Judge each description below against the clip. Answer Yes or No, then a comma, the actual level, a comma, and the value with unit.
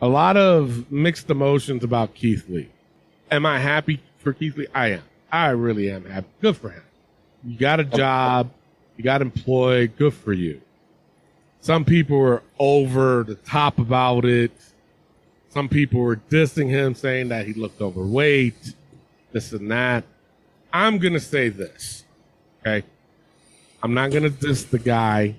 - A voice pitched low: Yes, low, 130 Hz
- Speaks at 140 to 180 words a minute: Yes, average, 160 wpm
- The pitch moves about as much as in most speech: Yes, average, 3.9 semitones